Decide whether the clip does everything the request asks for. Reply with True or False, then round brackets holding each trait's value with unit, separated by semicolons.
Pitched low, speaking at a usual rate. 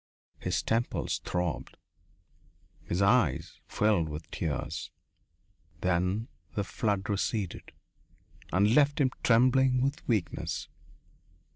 False (105 Hz; 95 wpm)